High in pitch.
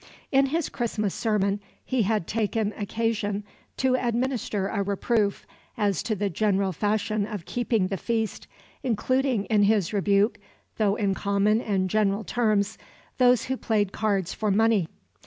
Yes: high, 210 Hz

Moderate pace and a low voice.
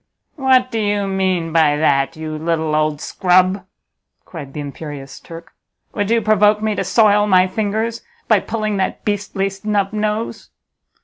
No: average, 150 wpm; high, 195 Hz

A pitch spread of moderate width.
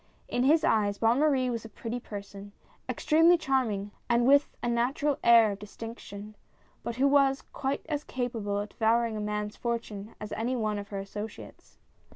Yes: average, 3.9 semitones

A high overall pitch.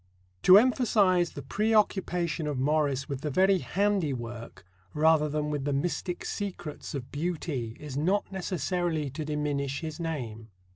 No: medium, 155 Hz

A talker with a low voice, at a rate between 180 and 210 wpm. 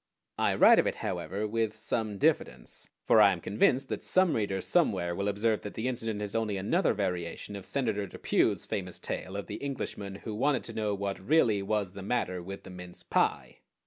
Yes: low, 105 Hz; average, 200 wpm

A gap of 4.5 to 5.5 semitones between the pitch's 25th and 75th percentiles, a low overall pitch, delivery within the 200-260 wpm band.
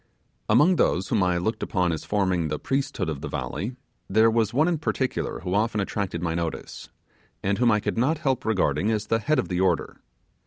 Yes: average, 5.2 semitones; low, 105 Hz; fast, 205 wpm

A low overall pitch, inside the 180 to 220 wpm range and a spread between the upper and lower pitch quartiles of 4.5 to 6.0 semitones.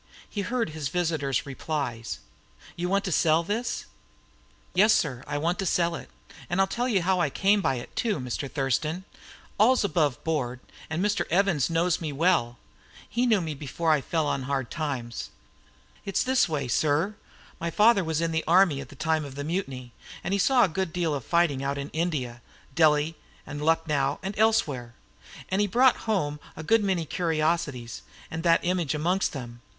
No: medium, 160 Hz; average, 185 wpm; average, 4.9 semitones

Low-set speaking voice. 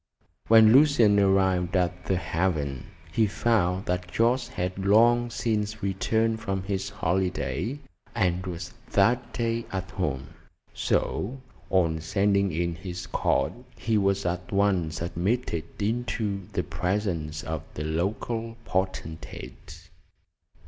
Yes: very low, 95 Hz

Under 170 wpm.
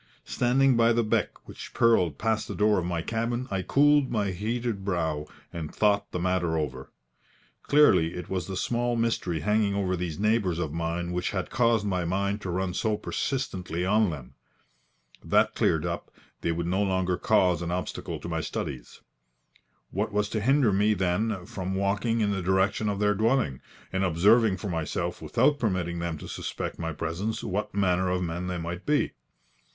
No: average, 180 wpm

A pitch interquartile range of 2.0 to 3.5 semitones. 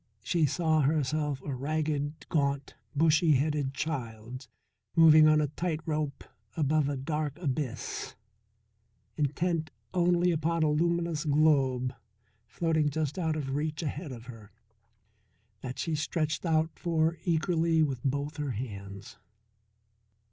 Yes: average, 2.7 semitones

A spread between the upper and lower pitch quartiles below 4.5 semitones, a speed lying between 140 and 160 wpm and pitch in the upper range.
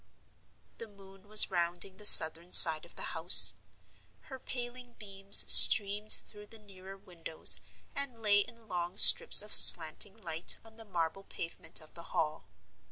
Yes: average, 4.1 semitones; average, 155 wpm; high, 195 Hz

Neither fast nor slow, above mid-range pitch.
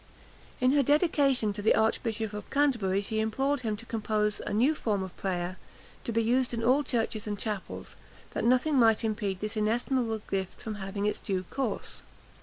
Yes: average, 185 wpm; high, 220 Hz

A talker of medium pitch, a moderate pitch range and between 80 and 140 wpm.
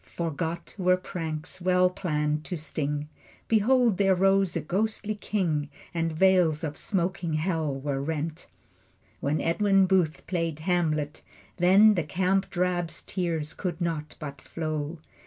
Yes: medium, 170 Hz; average, 3.4 semitones; slow, 135 wpm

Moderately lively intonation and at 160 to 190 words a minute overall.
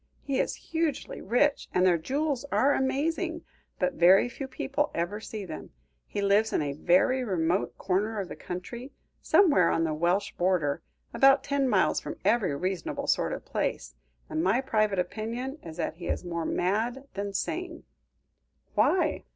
No: wide, 7.0 semitones; average, 165 wpm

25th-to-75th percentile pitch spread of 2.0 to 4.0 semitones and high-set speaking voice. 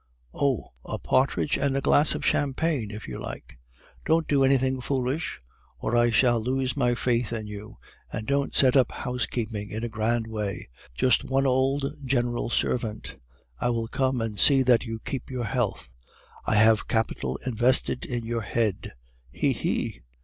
No: average, 3.0 semitones; low, 120 Hz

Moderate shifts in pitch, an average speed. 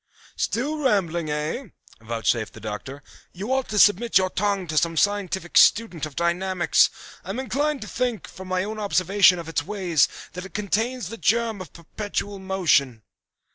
Yes: average, 4.4 semitones; average, 170 wpm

